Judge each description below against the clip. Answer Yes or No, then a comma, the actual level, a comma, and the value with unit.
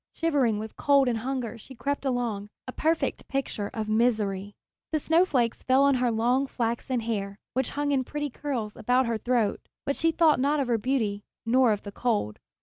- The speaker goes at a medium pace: Yes, average, 190 wpm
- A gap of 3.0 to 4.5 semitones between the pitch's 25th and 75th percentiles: Yes, average, 3.9 semitones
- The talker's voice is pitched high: Yes, high, 245 Hz